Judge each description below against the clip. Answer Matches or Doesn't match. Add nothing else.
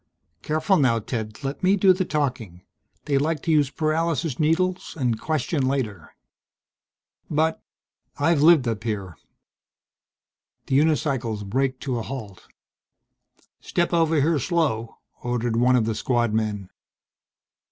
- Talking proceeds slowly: Matches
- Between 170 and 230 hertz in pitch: Doesn't match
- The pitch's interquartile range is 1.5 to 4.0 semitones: Doesn't match